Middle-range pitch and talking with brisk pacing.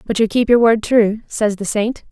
No: high, 220 Hz; fast, 255 wpm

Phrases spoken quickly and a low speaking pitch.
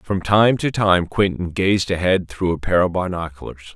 No: average, 190 wpm; very low, 90 Hz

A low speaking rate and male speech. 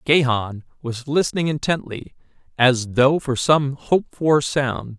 Yes: slow, 130 wpm; male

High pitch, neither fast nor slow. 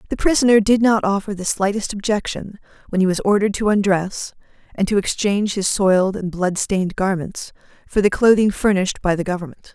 Yes: high, 200 Hz; average, 180 wpm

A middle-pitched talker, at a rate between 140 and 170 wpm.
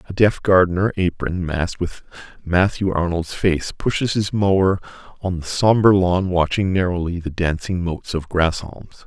No: very low, 90 Hz; average, 150 wpm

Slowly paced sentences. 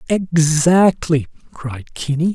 Yes: slow, 75 wpm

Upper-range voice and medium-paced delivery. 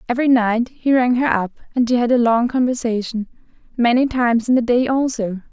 Yes: high, 240 Hz; average, 195 wpm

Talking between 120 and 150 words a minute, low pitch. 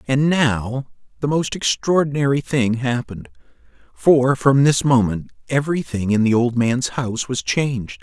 Yes: average, 140 wpm; low, 130 Hz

